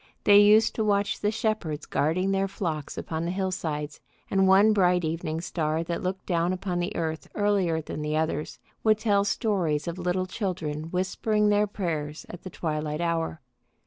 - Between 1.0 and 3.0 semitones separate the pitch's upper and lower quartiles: No, average, 4.0 semitones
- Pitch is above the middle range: No, medium, 180 Hz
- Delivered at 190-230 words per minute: No, average, 175 wpm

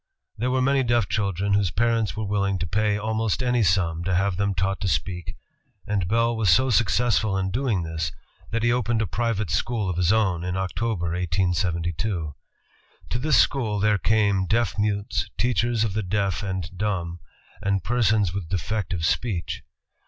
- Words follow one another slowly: No, average, 175 wpm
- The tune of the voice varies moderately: Yes, average, 3.7 semitones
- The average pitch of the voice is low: Yes, low, 100 Hz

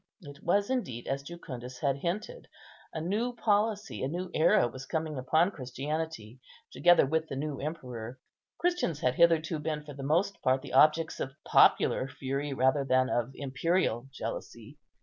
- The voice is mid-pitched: Yes, medium, 150 Hz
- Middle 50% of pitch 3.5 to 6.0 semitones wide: Yes, average, 4.5 semitones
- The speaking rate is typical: Yes, average, 160 wpm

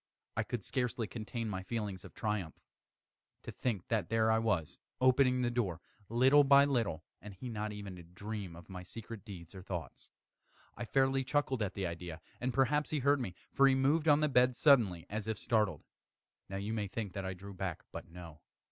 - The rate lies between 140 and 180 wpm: No, average, 200 wpm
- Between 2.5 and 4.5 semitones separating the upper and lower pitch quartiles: No, average, 5.2 semitones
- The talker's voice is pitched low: Yes, low, 110 Hz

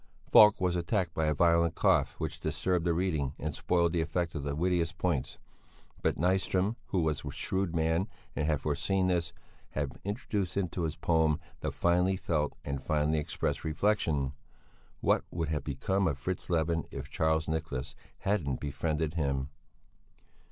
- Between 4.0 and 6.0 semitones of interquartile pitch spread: No, average, 3.2 semitones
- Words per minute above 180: No, average, 160 wpm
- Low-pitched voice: Yes, very low, 80 Hz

